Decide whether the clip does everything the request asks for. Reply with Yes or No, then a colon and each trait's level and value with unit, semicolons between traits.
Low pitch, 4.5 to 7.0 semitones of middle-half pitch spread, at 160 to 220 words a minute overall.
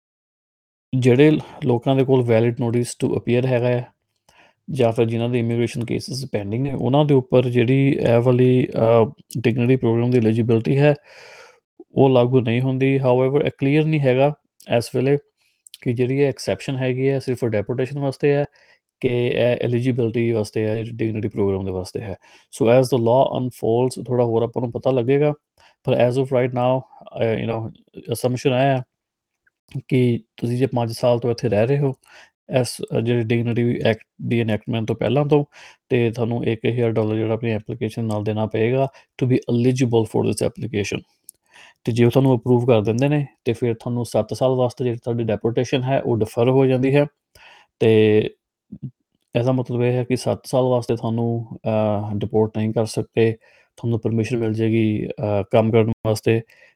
No: low, 120 Hz; narrow, 2.4 semitones; fast, 165 wpm